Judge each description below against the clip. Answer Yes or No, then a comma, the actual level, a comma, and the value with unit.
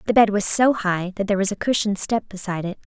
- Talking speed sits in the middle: No, fast, 265 wpm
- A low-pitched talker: No, high, 200 Hz